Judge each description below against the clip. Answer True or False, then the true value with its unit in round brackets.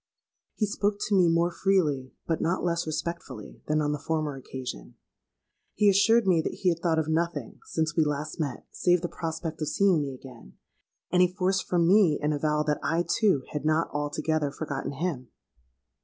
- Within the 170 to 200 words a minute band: True (185 wpm)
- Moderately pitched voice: True (160 Hz)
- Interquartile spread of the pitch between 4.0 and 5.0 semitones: False (3.2 semitones)